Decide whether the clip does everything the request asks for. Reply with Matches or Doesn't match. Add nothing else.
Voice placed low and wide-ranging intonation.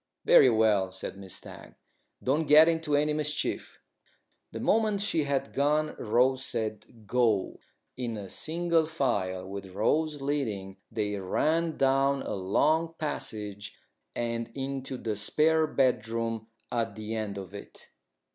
Matches